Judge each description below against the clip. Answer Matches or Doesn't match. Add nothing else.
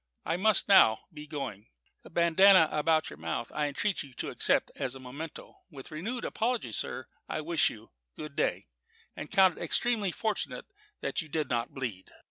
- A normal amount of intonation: Doesn't match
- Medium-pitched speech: Matches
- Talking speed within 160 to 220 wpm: Matches